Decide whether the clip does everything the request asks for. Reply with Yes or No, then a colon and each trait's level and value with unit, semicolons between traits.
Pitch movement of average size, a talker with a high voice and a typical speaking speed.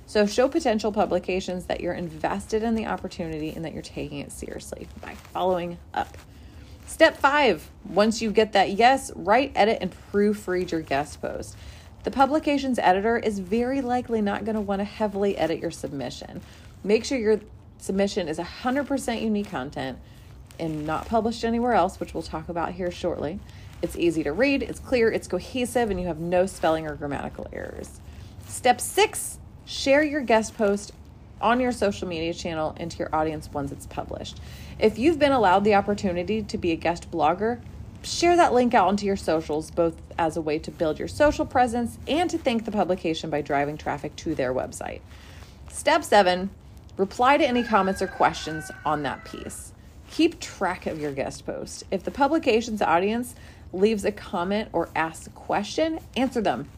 No: wide, 6.1 semitones; high, 205 Hz; average, 175 wpm